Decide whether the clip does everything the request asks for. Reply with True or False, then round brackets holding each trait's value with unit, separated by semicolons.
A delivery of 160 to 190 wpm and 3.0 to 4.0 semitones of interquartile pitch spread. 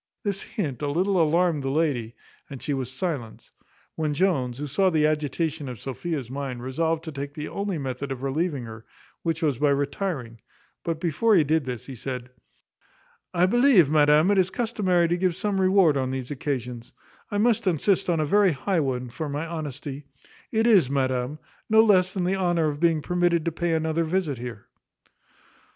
False (185 wpm; 4.9 semitones)